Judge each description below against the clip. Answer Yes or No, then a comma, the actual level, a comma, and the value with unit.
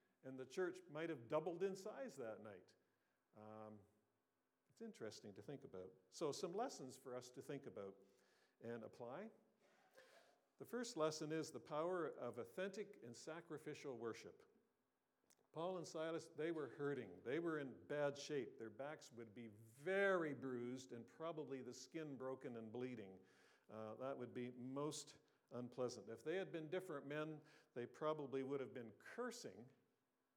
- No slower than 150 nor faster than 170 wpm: Yes, average, 155 wpm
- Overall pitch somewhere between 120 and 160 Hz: Yes, medium, 140 Hz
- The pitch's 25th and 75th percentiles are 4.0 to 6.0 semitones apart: Yes, average, 4.8 semitones